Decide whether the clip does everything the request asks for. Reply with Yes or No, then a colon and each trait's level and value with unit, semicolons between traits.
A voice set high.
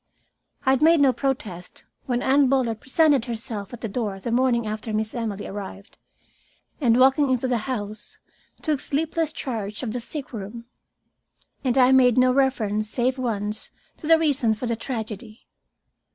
Yes: high, 245 Hz